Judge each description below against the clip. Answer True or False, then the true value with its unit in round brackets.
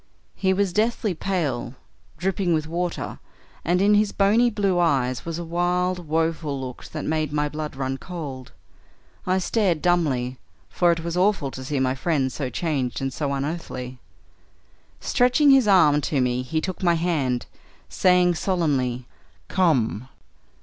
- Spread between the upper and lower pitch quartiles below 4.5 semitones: False (5.2 semitones)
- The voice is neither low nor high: True (165 Hz)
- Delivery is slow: False (150 wpm)